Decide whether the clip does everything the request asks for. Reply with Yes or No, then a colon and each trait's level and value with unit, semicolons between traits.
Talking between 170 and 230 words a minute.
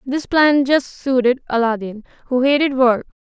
No: average, 150 wpm